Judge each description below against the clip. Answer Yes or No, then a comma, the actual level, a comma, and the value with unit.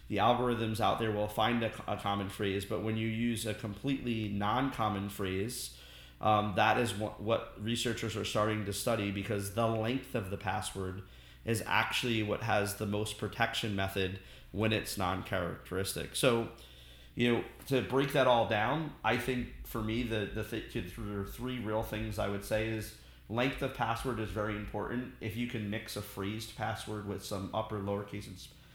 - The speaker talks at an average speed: Yes, average, 180 wpm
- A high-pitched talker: No, low, 110 Hz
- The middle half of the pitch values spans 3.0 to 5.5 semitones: No, narrow, 2.4 semitones